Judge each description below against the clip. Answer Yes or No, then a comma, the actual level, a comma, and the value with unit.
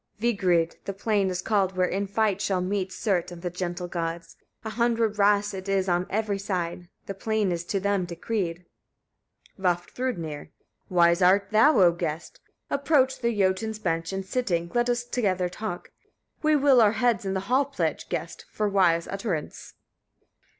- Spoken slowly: No, average, 175 wpm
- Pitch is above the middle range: Yes, high, 195 Hz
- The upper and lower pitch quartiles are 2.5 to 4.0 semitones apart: Yes, average, 3.7 semitones